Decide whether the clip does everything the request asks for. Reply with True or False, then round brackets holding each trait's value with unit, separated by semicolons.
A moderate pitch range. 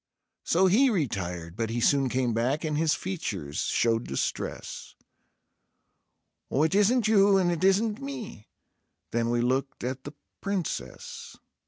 False (8.7 semitones)